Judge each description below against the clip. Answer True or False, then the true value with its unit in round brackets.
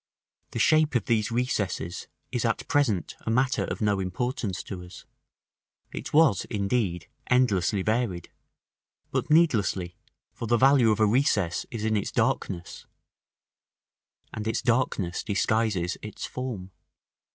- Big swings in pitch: False (4.7 semitones)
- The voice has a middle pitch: False (110 Hz)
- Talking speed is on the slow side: True (130 wpm)